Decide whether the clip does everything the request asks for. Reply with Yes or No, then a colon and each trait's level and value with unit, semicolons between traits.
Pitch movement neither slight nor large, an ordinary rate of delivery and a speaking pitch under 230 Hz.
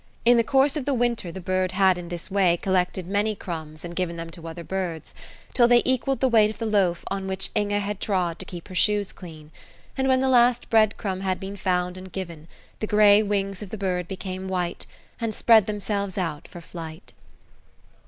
No: average, 3.1 semitones; fast, 210 wpm; high, 190 Hz